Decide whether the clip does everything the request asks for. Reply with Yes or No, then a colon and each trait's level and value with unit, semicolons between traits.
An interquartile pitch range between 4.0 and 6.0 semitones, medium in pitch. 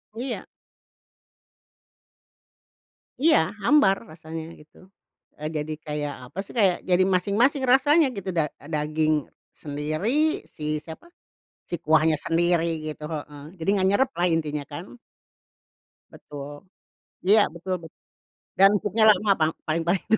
Yes: average, 5.1 semitones; medium, 170 Hz